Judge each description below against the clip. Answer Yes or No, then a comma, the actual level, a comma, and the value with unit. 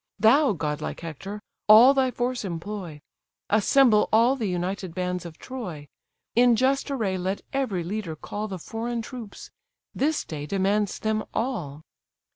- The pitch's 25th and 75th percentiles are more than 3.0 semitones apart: Yes, average, 5.2 semitones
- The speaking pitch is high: Yes, high, 210 Hz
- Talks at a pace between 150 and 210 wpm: No, average, 140 wpm